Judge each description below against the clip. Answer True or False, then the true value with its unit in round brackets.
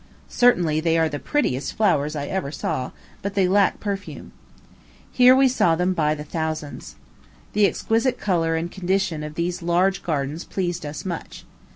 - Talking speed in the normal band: True (160 wpm)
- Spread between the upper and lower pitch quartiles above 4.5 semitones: False (4.0 semitones)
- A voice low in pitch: False (175 Hz)